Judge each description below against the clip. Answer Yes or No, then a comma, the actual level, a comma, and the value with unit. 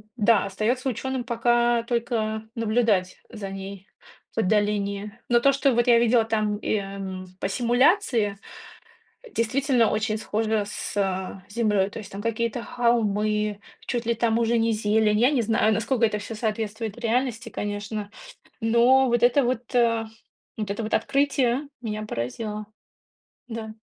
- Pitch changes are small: Yes, narrow, 2.2 semitones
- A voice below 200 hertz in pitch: No, high, 225 Hz